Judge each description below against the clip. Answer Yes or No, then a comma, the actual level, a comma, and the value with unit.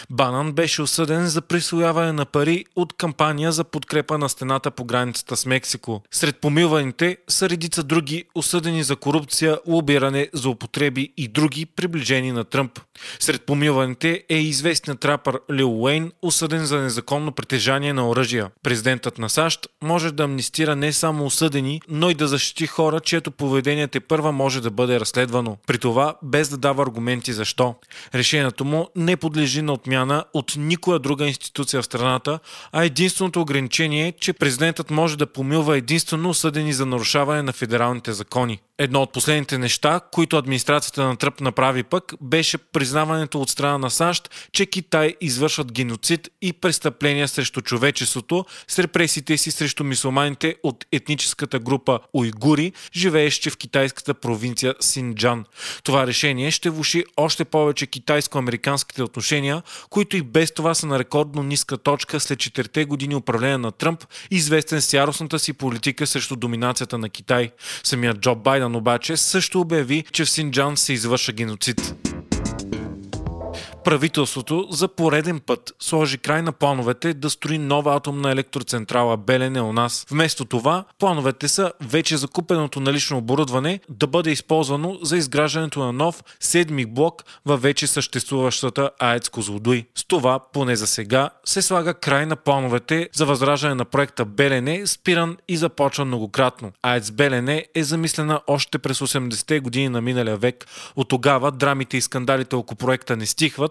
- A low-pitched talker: No, medium, 145 Hz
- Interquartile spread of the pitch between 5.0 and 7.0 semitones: No, average, 3.6 semitones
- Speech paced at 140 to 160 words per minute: Yes, average, 150 wpm